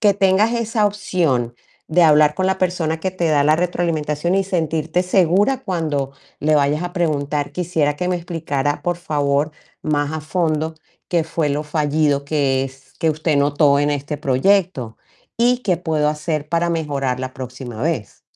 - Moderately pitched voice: Yes, medium, 155 Hz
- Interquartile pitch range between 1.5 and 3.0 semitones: No, average, 3.5 semitones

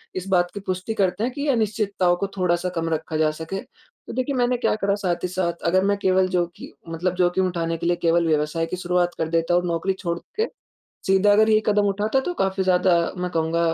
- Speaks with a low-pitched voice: No, medium, 185 Hz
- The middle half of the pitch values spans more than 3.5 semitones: No, average, 2.9 semitones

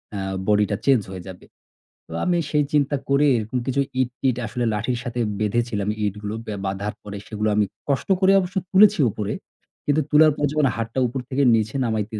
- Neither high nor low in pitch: No, low, 120 Hz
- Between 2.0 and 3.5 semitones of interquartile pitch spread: No, average, 5.1 semitones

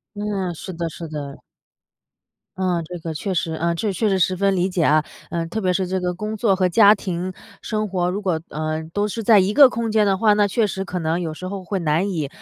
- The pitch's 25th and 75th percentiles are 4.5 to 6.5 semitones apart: No, average, 3.3 semitones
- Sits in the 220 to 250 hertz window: No, medium, 185 Hz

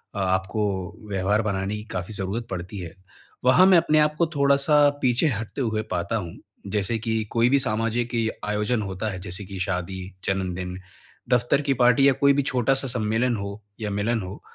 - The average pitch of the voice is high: No, low, 110 Hz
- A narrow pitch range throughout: No, average, 4.4 semitones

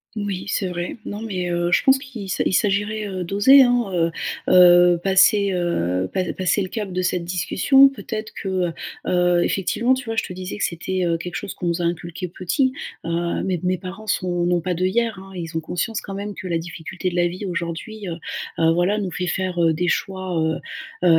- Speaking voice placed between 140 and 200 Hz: Yes, medium, 185 Hz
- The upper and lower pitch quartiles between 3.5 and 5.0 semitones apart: No, average, 2.8 semitones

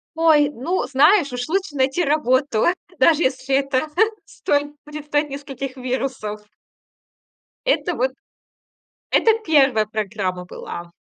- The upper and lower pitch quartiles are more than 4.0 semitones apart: No, average, 3.2 semitones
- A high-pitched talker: Yes, very high, 275 Hz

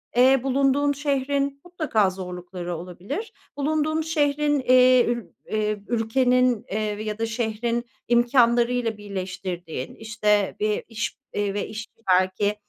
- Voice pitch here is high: Yes, high, 235 Hz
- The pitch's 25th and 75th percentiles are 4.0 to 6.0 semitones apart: Yes, average, 4.6 semitones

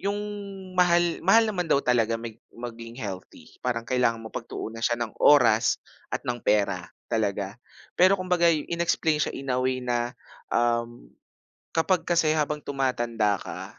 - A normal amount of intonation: No, wide, 6.1 semitones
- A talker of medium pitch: No, low, 125 Hz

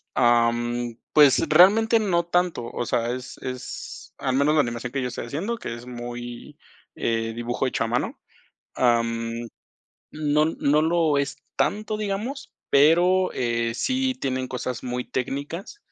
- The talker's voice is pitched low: Yes, low, 130 Hz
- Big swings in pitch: Yes, wide, 6.2 semitones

